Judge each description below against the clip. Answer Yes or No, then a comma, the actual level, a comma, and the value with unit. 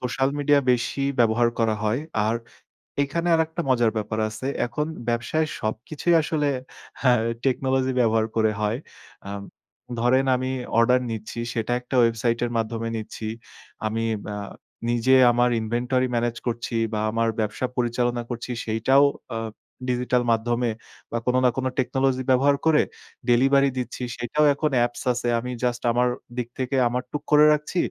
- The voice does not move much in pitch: Yes, narrow, 2.3 semitones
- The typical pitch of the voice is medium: No, low, 120 Hz